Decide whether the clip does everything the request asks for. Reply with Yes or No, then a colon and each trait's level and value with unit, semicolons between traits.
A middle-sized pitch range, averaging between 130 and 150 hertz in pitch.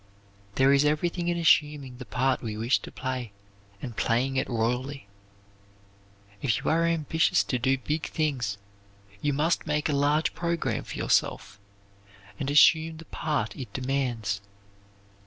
Yes: average, 3.8 semitones; medium, 140 Hz